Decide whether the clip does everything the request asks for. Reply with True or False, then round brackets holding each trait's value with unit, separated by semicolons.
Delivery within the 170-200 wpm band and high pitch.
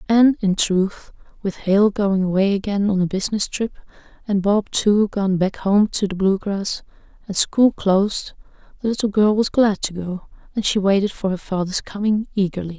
True (185 wpm; 200 Hz)